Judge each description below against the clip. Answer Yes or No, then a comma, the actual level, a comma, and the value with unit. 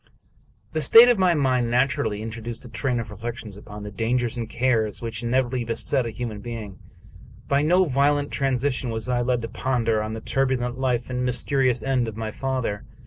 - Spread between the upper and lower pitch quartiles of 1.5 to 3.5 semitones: Yes, average, 2.8 semitones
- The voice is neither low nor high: No, low, 120 Hz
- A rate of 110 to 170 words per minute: No, average, 195 wpm